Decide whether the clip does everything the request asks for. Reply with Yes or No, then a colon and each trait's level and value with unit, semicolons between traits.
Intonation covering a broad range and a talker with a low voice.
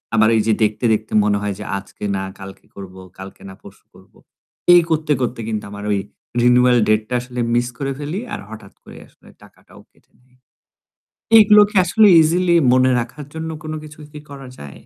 Yes: wide, 6.5 semitones; low, 125 Hz